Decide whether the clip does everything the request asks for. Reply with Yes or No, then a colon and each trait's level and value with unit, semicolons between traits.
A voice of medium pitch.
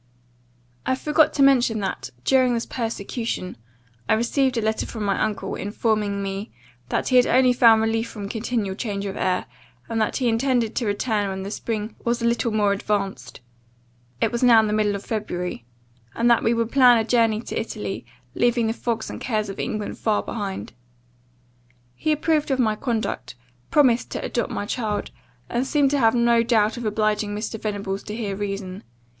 No: high, 225 Hz